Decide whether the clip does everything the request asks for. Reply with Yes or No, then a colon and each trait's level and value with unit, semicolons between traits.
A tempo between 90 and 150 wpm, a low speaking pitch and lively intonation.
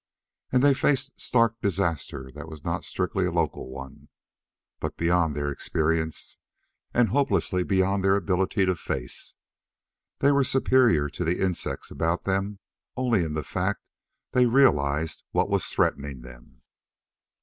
Yes: average, 140 wpm; very low, 90 Hz; wide, 5.9 semitones